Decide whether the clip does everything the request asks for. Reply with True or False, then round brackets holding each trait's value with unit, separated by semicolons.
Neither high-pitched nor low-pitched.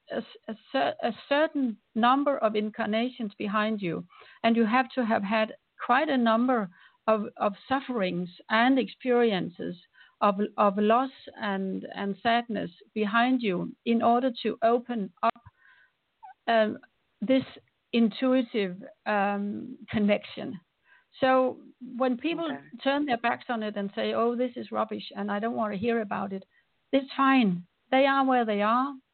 False (230 Hz)